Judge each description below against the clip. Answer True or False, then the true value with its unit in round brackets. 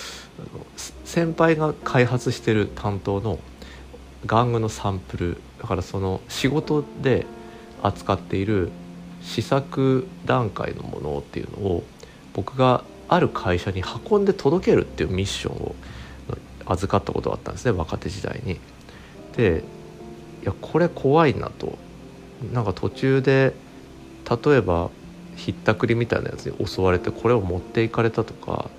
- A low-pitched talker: True (110 Hz)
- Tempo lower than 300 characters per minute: True (275 characters per minute)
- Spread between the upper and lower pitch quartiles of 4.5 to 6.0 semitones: True (5.4 semitones)